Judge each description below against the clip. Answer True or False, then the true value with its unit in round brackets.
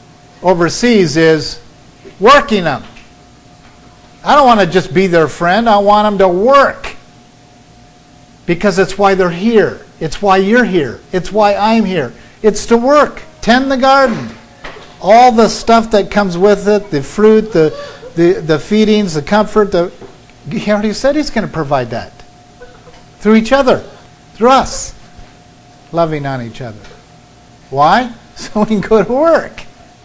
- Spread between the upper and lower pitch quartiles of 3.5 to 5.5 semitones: True (4.8 semitones)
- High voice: True (205 Hz)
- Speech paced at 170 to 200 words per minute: False (150 wpm)